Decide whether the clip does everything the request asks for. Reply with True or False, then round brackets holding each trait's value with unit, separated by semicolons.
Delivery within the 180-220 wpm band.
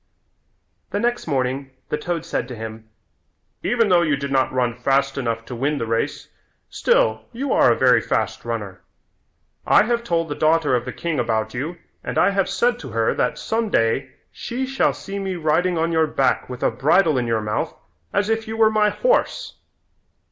True (195 wpm)